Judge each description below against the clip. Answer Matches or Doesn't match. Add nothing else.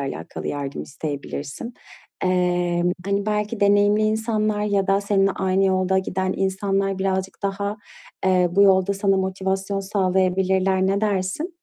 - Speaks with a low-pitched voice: Doesn't match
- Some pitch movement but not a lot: Doesn't match